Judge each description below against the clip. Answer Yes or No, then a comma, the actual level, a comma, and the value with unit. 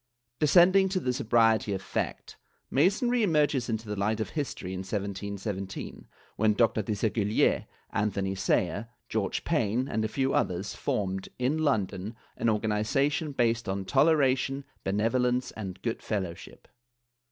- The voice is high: No, low, 110 Hz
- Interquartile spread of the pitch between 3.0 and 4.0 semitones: No, average, 5.2 semitones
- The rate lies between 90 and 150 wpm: Yes, average, 140 wpm